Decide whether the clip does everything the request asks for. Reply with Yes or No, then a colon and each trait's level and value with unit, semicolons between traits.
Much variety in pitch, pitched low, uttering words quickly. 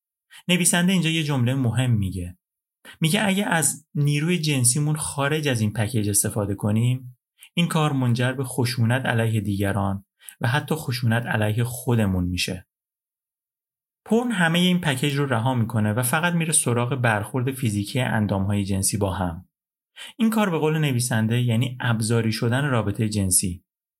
No: wide, 5.9 semitones; low, 125 Hz; average, 145 wpm